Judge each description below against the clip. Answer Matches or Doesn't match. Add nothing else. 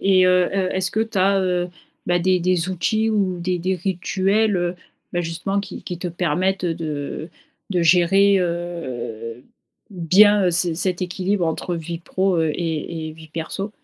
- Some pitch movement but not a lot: Doesn't match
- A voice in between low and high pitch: Matches